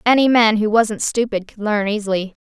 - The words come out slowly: No, average, 195 wpm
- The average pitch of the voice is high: Yes, high, 215 Hz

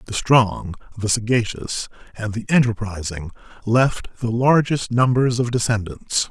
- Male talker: Yes, male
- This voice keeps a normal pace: No, slow, 125 wpm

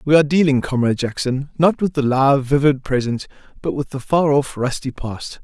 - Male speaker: Yes, male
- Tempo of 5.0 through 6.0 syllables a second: Yes, 5.3 syllables/s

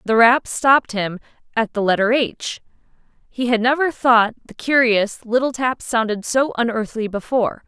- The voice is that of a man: No, female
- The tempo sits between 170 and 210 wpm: No, average, 155 wpm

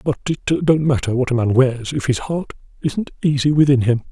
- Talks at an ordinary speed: No, fast, 220 wpm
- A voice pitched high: No, low, 135 Hz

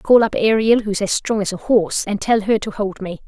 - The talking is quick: Yes, fast, 295 wpm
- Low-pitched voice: No, high, 205 Hz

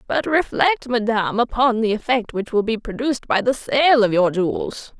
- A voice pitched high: Yes, high, 235 Hz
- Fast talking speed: No, average, 190 wpm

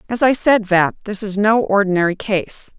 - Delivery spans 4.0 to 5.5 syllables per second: Yes, 4.9 syllables/s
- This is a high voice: Yes, high, 205 Hz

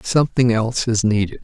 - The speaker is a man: Yes, male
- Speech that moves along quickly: No, average, 165 wpm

